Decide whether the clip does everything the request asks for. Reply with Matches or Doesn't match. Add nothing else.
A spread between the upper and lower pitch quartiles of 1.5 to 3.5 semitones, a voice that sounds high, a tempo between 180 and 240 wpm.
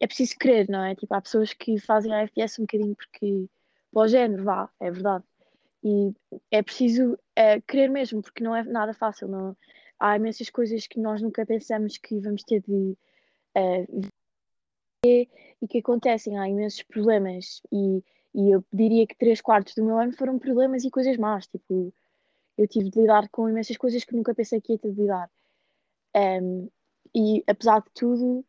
Matches